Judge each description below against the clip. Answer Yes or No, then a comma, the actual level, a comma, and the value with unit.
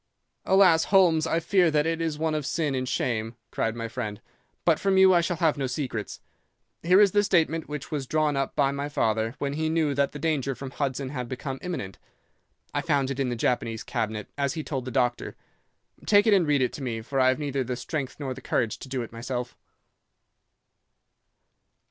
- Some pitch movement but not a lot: Yes, average, 4.2 semitones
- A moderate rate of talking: No, fast, 210 wpm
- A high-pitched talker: No, medium, 140 Hz